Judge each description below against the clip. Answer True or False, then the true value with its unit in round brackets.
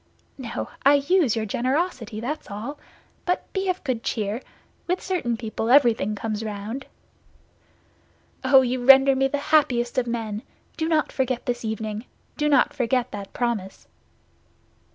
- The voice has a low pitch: False (245 Hz)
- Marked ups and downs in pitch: False (4.2 semitones)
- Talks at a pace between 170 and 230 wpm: False (140 wpm)